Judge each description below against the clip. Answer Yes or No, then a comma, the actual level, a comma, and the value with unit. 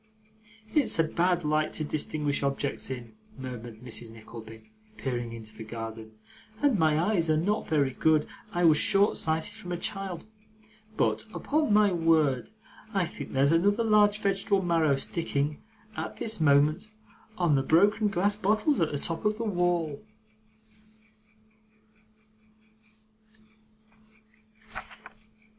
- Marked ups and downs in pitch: Yes, wide, 6.0 semitones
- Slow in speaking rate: Yes, slow, 130 wpm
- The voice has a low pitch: No, medium, 160 Hz